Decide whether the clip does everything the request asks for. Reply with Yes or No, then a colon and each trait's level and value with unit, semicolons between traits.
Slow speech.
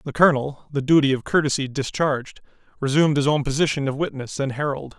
No: average, 180 wpm